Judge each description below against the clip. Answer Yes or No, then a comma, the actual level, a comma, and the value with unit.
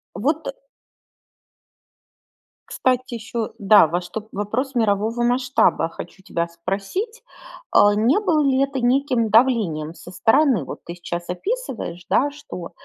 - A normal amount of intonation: No, wide, 6.1 semitones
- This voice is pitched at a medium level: No, high, 225 Hz